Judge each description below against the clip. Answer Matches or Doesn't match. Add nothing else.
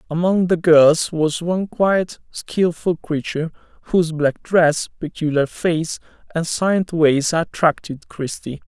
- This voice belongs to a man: Matches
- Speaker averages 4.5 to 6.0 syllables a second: Doesn't match